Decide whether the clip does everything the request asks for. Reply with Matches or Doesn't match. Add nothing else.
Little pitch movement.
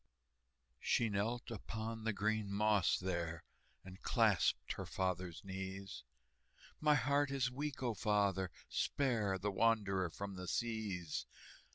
Doesn't match